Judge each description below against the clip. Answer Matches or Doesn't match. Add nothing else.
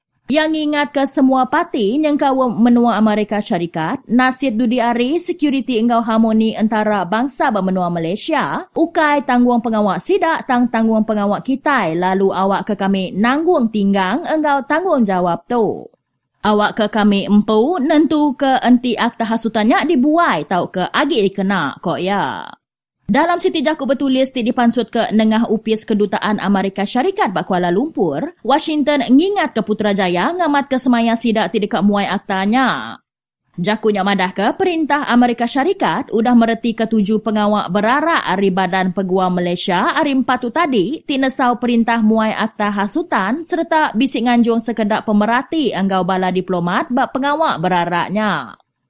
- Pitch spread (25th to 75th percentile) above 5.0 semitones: Matches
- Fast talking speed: Doesn't match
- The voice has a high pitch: Matches